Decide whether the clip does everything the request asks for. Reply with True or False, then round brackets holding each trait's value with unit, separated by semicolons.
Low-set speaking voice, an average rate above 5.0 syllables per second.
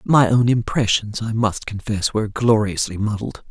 False (110 Hz; 4.7 syllables/s)